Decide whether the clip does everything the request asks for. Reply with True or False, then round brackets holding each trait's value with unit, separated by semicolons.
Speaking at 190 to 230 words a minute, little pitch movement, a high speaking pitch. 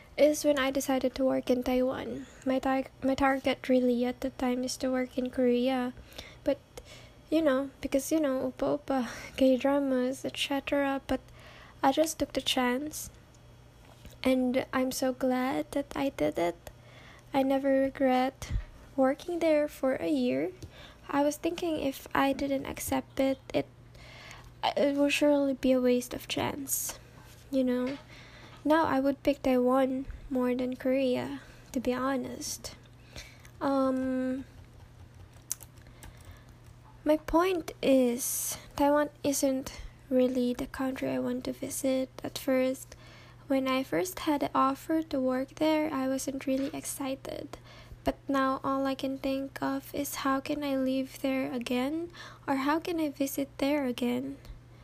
False (145 wpm; 1.6 semitones; 265 Hz)